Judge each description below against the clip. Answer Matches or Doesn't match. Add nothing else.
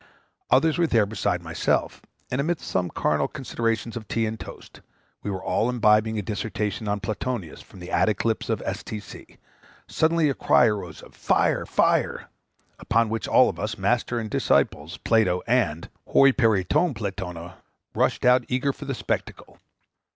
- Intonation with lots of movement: Doesn't match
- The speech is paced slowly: Doesn't match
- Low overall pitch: Matches